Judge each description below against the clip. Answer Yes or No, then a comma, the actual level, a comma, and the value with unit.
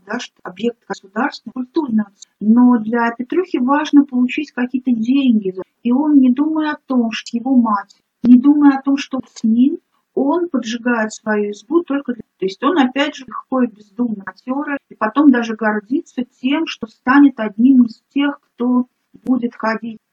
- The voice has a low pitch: No, very high, 250 Hz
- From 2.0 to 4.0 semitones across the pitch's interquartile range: Yes, average, 3.6 semitones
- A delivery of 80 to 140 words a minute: No, fast, 160 wpm